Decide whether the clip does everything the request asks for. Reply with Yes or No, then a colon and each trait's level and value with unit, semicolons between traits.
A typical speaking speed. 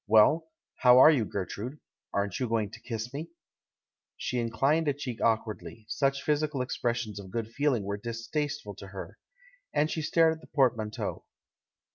Yes: average, 170 wpm